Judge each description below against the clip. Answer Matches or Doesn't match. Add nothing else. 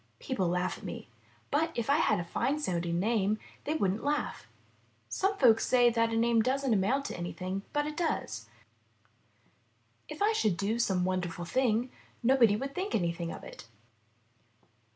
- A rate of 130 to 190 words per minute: Matches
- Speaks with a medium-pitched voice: Doesn't match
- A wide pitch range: Matches